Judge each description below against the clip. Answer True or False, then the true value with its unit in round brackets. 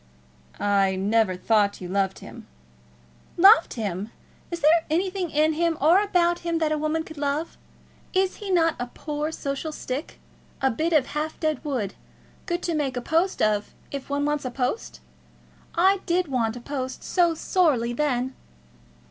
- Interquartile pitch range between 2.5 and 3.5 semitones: False (5.6 semitones)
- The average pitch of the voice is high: True (300 Hz)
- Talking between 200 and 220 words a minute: False (165 wpm)